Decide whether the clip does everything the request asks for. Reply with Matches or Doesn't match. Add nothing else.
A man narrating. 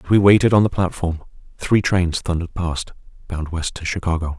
Matches